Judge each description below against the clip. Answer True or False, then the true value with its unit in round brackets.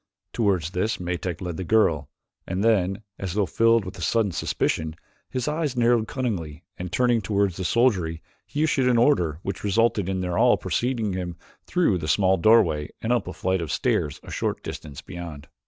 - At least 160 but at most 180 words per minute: False (190 wpm)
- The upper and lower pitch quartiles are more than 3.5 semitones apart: True (4.9 semitones)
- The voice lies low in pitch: True (95 Hz)